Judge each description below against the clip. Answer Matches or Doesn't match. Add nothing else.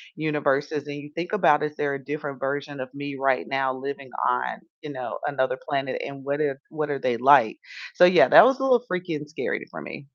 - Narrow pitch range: Matches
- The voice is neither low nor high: Matches